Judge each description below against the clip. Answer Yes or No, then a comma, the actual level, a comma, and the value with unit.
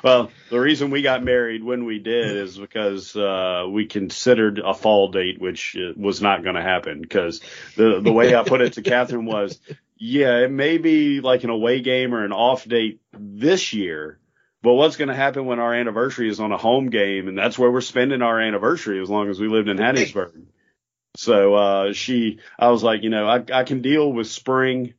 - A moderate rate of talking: No, fast, 210 wpm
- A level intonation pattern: No, average, 3.5 semitones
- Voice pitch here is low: Yes, low, 115 Hz